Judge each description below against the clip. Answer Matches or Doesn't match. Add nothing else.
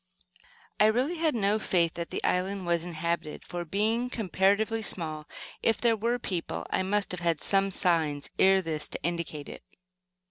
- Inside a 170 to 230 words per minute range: Matches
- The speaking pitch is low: Doesn't match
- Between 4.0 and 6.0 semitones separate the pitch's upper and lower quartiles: Matches